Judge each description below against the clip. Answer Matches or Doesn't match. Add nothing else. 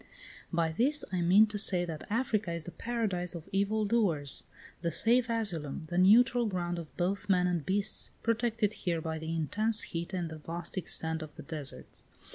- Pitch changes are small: Doesn't match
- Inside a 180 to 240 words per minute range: Matches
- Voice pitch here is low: Doesn't match